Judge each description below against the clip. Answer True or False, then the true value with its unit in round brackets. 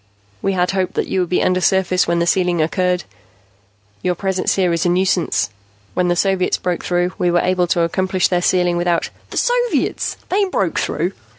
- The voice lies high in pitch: False (180 Hz)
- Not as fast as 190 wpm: False (195 wpm)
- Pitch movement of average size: False (1.2 semitones)